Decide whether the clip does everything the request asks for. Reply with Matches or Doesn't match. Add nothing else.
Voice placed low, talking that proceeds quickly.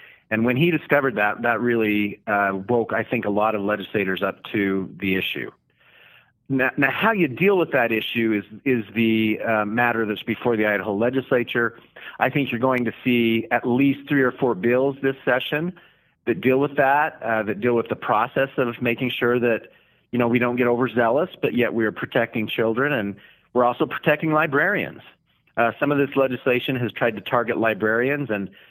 Doesn't match